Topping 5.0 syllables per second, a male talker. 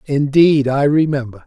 No: 4.5 syllables/s; male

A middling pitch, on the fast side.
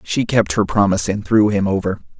No: low, 100 Hz; fast, 220 wpm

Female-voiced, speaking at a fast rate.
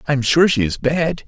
No: male; fast, 285 wpm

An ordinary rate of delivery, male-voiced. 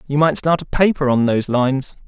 No: fast, 230 wpm; male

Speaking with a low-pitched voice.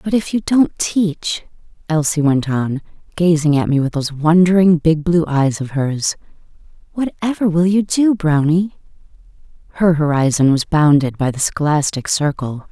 No: medium, 160 Hz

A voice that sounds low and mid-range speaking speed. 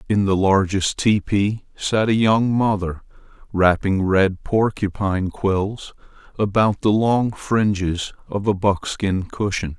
No: low, 100 Hz; slow, 125 wpm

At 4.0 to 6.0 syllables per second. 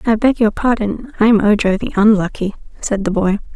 Yes: 5.2 syllables/s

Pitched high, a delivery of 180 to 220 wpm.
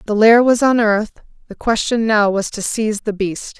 Yes: high, 215 Hz; average, 200 wpm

